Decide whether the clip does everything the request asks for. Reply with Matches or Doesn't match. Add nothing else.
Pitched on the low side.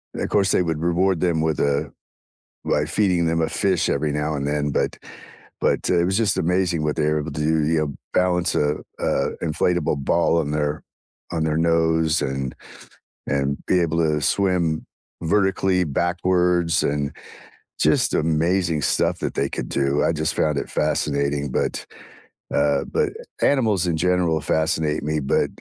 Matches